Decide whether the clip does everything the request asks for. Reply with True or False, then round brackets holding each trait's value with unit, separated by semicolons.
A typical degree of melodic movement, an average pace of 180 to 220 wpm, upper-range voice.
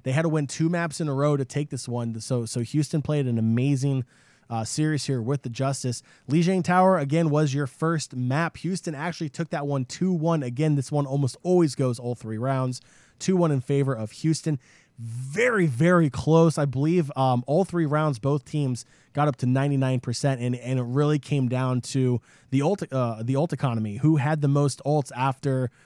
False (3.5 semitones; 205 wpm; 140 Hz)